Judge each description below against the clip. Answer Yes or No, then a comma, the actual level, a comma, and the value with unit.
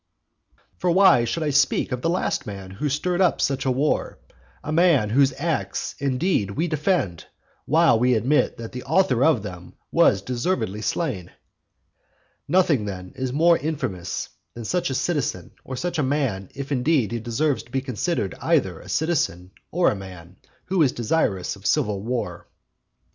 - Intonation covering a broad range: Yes, wide, 7.5 semitones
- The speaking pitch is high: No, low, 130 Hz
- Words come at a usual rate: Yes, average, 170 wpm